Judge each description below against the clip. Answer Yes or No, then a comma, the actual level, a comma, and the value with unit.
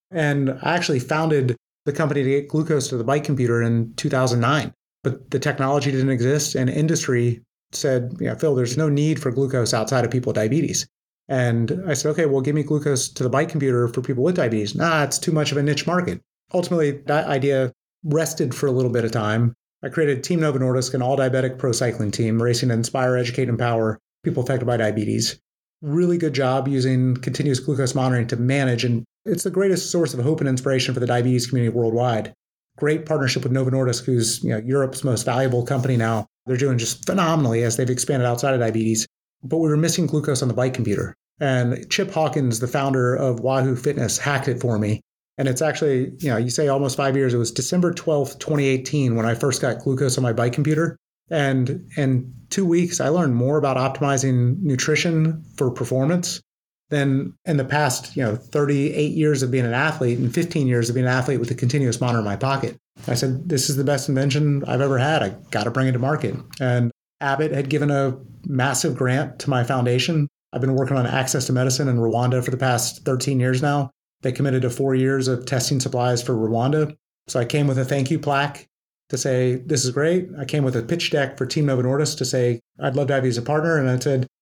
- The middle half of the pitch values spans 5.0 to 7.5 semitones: No, average, 2.9 semitones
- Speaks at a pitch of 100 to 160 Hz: Yes, low, 135 Hz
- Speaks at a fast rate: Yes, fast, 215 wpm